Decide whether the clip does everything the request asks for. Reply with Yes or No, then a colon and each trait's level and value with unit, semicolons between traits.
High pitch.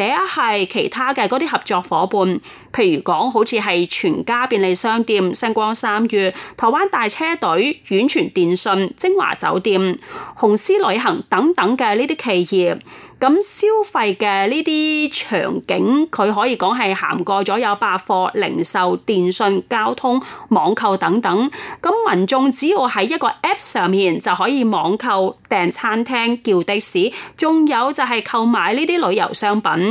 Yes: high, 230 Hz